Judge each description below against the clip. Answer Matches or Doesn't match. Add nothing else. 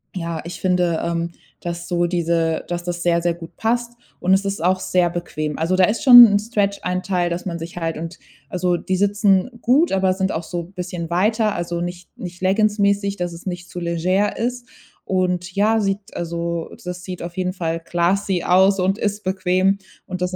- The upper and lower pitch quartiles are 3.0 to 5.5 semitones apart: Doesn't match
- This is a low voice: Doesn't match